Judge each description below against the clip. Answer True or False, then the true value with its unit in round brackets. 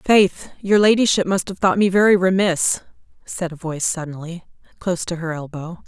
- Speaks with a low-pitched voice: False (180 Hz)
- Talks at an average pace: True (175 wpm)